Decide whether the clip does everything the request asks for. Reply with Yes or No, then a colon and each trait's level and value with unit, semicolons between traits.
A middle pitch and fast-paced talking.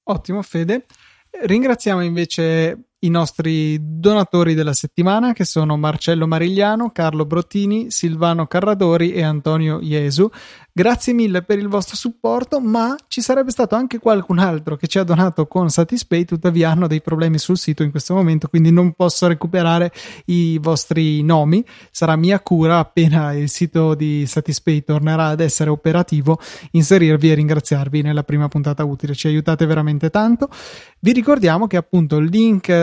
No: medium, 170 Hz; average, 155 wpm